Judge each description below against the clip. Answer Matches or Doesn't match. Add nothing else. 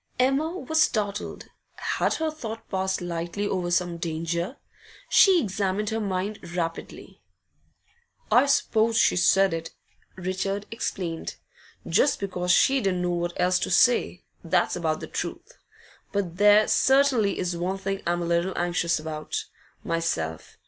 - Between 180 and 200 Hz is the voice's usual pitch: Matches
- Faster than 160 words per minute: Doesn't match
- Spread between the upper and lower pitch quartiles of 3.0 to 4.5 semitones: Matches